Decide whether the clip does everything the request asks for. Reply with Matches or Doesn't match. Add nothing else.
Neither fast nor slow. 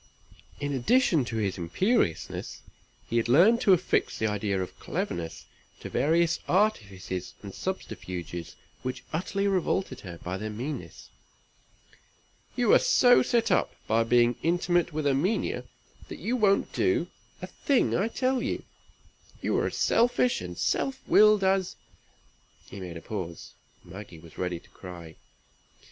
Matches